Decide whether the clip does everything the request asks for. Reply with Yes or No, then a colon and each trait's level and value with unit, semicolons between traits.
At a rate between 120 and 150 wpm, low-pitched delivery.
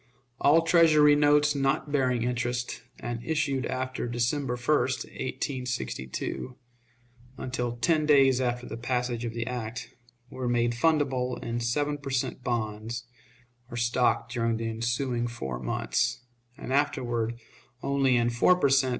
Yes: slow, 135 wpm; low, 125 Hz